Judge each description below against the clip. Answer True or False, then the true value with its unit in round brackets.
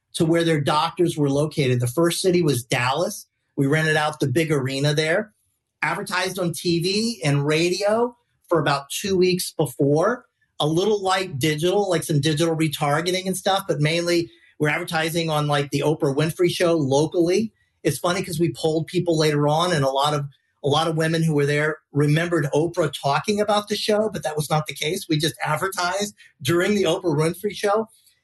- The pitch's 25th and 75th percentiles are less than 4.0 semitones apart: True (3.2 semitones)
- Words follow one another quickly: False (185 wpm)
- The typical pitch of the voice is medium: True (160 Hz)